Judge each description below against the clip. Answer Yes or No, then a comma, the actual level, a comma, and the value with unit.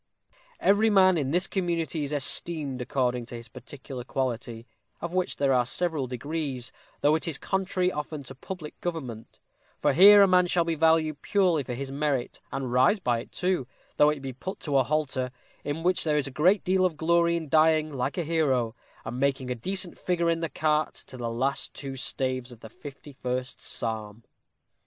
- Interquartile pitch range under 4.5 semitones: No, average, 4.8 semitones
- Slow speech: No, average, 195 wpm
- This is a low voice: No, medium, 145 Hz